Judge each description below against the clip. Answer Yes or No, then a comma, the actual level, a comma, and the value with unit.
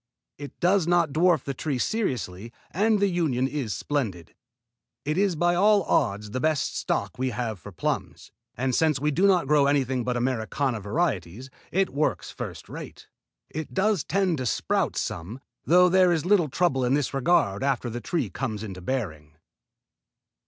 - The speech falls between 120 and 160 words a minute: No, average, 170 wpm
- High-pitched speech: No, medium, 140 Hz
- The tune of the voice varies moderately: No, wide, 6.3 semitones